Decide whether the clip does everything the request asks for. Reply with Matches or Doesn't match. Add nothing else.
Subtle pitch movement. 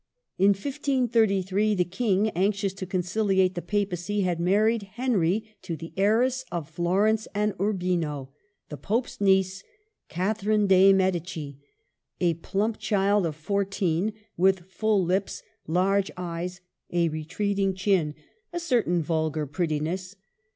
Doesn't match